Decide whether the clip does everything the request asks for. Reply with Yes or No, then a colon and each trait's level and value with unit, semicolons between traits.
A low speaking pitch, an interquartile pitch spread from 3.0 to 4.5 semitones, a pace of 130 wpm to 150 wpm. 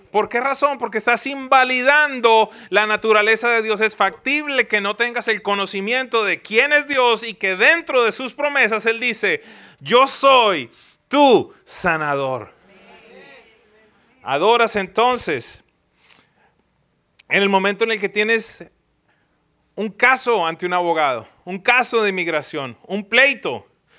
No: high, 225 Hz; average, 4.1 semitones; slow, 135 wpm